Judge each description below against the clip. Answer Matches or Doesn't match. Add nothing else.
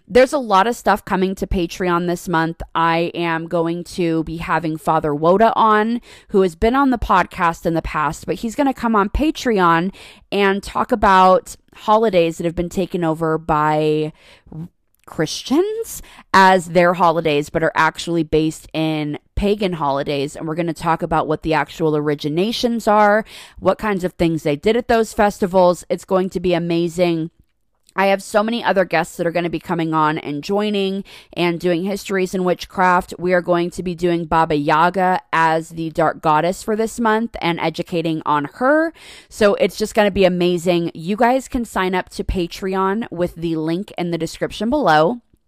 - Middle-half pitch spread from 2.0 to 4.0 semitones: Matches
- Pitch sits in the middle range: Matches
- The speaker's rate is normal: Matches